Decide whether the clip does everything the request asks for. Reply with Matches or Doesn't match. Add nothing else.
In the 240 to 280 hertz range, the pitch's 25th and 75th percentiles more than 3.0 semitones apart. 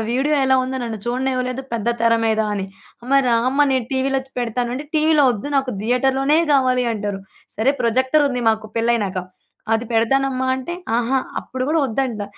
Doesn't match